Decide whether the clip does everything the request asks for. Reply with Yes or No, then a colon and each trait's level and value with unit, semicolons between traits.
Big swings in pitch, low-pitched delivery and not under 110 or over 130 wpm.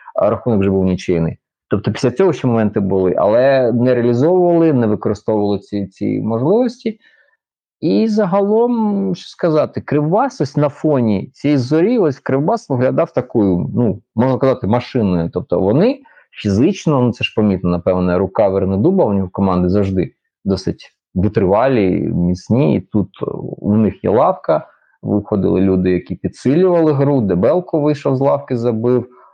No: wide, 7.4 semitones; low, 120 Hz; average, 145 wpm